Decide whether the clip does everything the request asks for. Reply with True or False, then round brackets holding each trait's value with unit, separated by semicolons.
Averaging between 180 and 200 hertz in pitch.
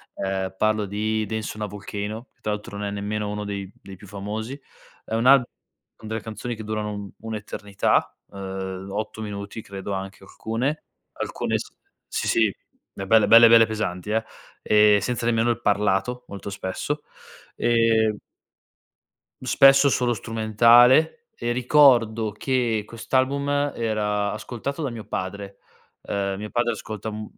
False (110 Hz)